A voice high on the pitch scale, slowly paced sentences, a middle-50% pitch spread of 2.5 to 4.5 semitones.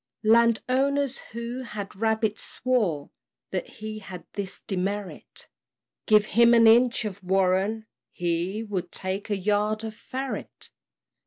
Yes: high, 215 Hz; slow, 130 wpm; average, 3.3 semitones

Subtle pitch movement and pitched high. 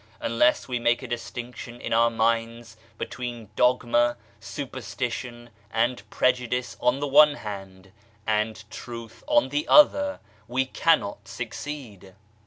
No: narrow, 2.0 semitones; low, 120 Hz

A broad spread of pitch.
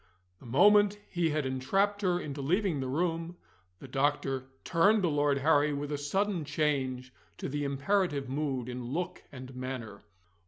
No: average, 4.9 semitones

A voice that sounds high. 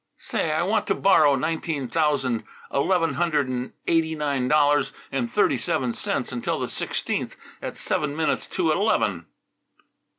No: medium, 150 Hz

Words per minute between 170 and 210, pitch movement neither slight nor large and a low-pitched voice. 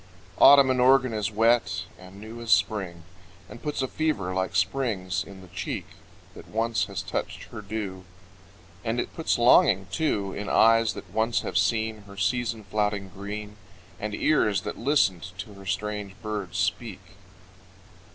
No: average, 160 wpm; average, 3.3 semitones; low, 105 Hz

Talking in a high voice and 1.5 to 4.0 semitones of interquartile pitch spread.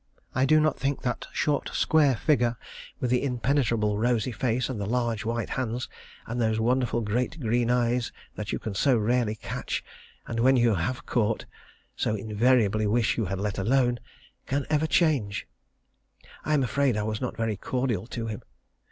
No: low, 120 Hz; average, 2.9 semitones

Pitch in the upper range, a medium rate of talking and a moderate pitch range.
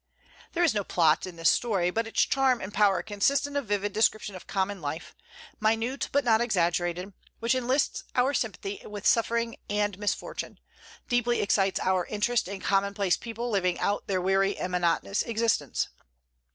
Yes: high, 205 Hz; average, 165 wpm; average, 3.6 semitones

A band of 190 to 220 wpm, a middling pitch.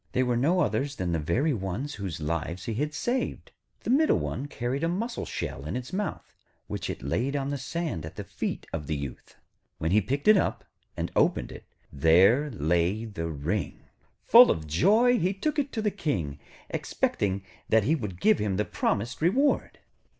No: average, 195 wpm; low, 115 Hz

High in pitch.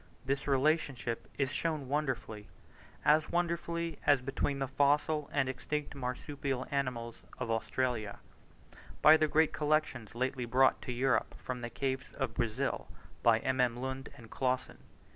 No: low, 135 Hz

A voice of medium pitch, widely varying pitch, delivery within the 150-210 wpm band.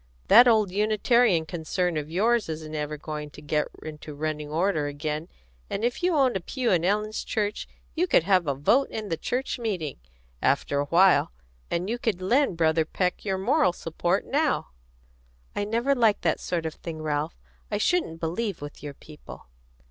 Yes: medium, 180 Hz; wide, 6.0 semitones; average, 180 wpm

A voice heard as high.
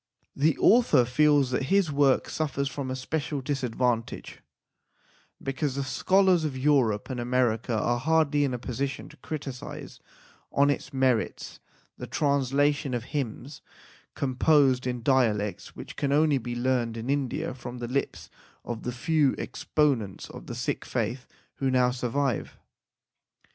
No: low, 130 Hz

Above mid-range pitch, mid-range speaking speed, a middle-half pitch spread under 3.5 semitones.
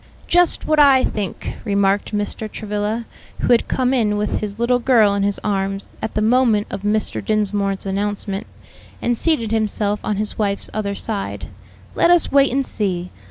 Yes: high, 210 Hz; average, 170 wpm; average, 2.8 semitones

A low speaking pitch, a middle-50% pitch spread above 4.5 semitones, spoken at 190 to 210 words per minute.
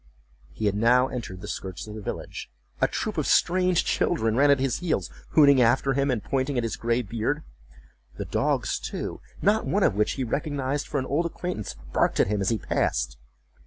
Yes: low, 130 Hz; average, 4.9 semitones; average, 200 wpm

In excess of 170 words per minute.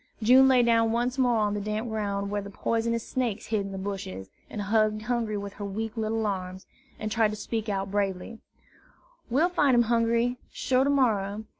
Yes: average, 195 wpm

